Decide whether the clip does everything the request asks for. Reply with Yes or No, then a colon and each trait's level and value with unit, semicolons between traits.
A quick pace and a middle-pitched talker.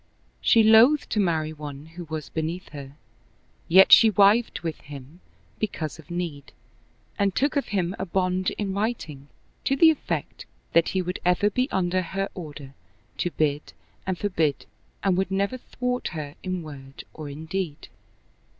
No: average, 160 wpm; medium, 180 Hz